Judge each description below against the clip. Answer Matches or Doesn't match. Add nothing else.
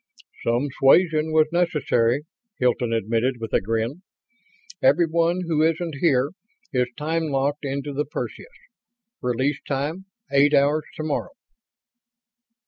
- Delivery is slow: Matches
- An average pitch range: Matches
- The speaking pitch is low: Doesn't match